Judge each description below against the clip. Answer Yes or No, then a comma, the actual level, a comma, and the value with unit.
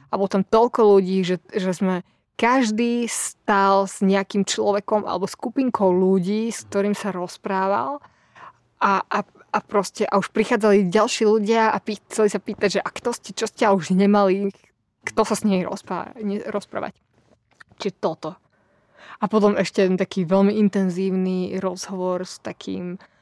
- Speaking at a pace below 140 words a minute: No, average, 160 wpm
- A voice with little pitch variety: Yes, narrow, 2.1 semitones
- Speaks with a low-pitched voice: No, high, 200 Hz